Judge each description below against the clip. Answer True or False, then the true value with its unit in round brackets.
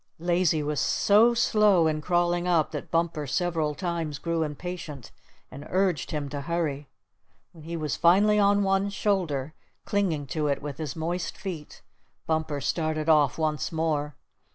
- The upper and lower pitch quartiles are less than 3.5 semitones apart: True (3.1 semitones)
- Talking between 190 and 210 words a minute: False (155 wpm)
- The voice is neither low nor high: True (160 Hz)